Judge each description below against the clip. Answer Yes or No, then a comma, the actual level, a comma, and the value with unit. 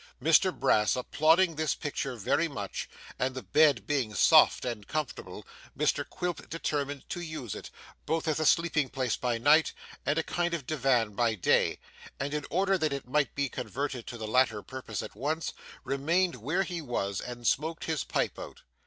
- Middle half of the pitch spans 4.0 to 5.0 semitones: Yes, average, 4.5 semitones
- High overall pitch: No, medium, 140 Hz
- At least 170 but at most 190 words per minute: Yes, average, 185 wpm